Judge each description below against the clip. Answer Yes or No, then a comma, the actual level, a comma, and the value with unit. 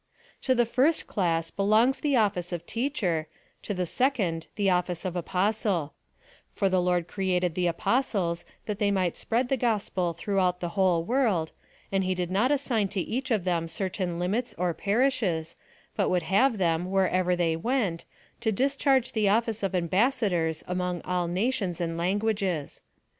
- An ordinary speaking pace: Yes, average, 170 wpm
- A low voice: No, high, 190 Hz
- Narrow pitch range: No, average, 4.3 semitones